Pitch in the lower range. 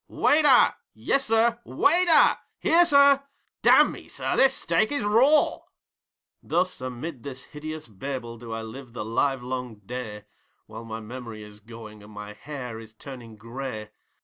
Yes: low, 125 Hz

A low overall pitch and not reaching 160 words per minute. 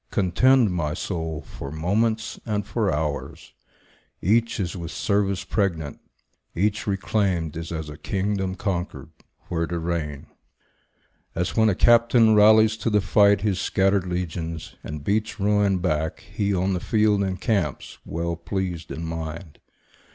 Yes: very low, 95 Hz; average, 140 wpm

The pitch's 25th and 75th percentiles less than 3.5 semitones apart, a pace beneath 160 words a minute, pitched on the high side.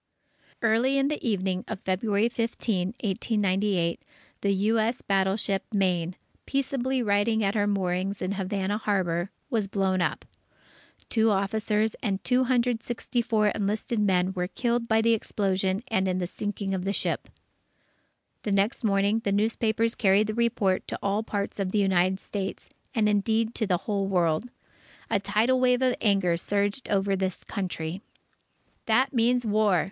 Yes: average, 2.8 semitones; average, 150 wpm; high, 205 Hz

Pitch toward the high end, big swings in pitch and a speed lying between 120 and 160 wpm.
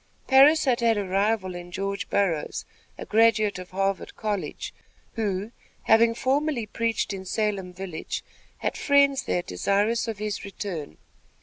No: high, 205 Hz; average, 3.4 semitones; average, 140 wpm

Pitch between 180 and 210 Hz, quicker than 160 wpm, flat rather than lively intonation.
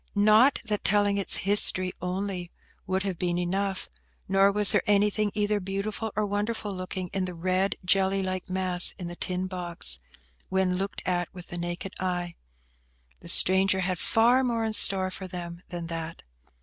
Yes: high, 190 Hz; average, 170 wpm; narrow, 2.1 semitones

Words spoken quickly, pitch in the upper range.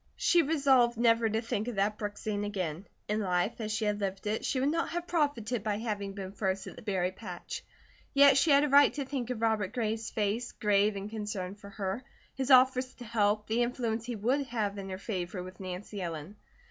Yes: fast, 220 wpm; high, 215 Hz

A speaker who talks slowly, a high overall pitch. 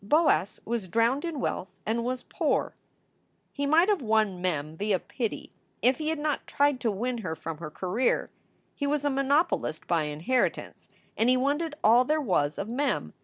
No: average, 180 wpm; high, 240 Hz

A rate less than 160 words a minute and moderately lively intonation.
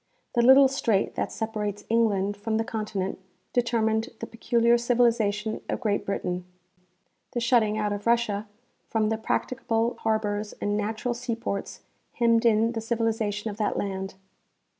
No: average, 140 wpm; narrow, 2.1 semitones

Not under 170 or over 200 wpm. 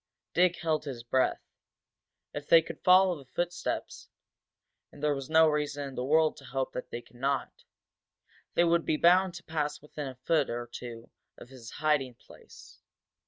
Yes: average, 175 wpm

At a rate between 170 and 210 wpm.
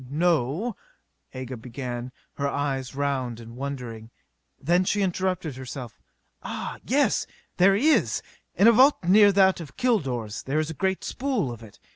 No: average, 155 wpm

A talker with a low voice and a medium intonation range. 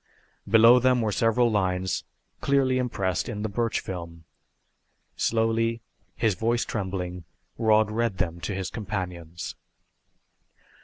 Yes: low, 105 Hz; average, 3.8 semitones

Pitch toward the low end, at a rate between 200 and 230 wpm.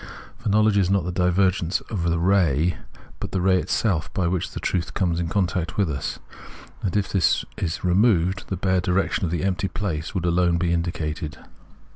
No: very low, 90 Hz; average, 190 wpm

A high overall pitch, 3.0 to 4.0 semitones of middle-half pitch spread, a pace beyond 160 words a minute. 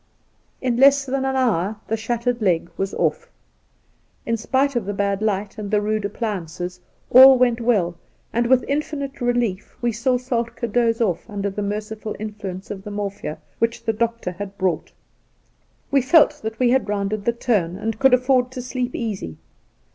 Yes: high, 225 Hz; average, 3.6 semitones; average, 175 wpm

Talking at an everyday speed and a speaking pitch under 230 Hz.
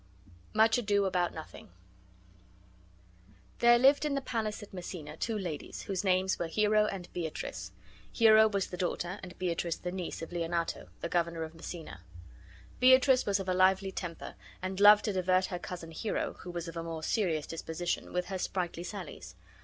Yes: average, 175 wpm; medium, 185 Hz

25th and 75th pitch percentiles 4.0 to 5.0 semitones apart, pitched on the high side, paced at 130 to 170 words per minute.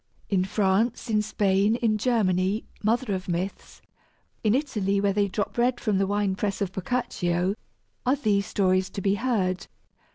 No: narrow, 2.6 semitones; high, 200 Hz; average, 160 wpm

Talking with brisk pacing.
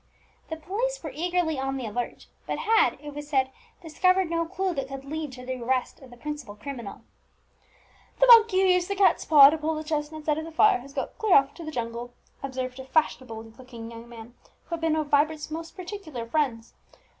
Yes: fast, 215 wpm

